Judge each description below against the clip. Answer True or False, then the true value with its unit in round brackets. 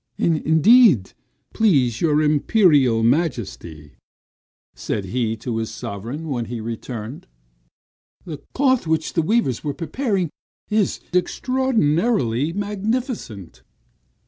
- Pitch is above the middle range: False (150 Hz)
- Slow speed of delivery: True (95 wpm)